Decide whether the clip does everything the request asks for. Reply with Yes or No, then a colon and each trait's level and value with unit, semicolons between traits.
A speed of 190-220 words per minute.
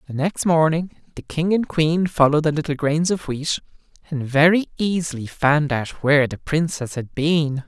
No: average, 180 wpm